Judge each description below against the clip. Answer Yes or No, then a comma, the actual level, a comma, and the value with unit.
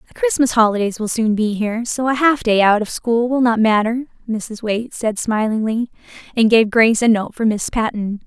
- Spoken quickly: Yes, fast, 210 wpm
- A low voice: No, high, 225 Hz